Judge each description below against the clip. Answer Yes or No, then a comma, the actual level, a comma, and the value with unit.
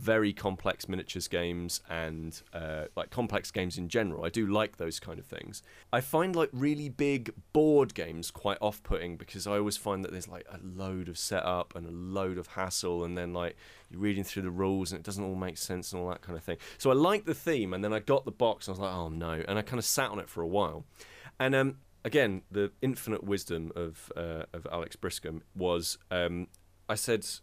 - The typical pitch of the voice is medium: No, very low, 95 Hz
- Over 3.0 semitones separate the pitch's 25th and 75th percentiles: Yes, average, 3.6 semitones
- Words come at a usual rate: No, fast, 230 wpm